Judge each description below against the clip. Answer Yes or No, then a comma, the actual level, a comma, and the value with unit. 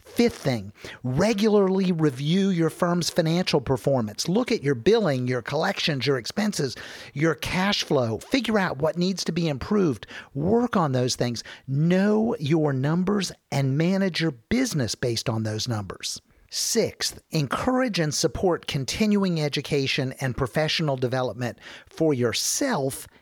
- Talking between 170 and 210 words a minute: No, slow, 135 wpm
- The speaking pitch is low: No, medium, 155 Hz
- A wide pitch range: Yes, wide, 6.4 semitones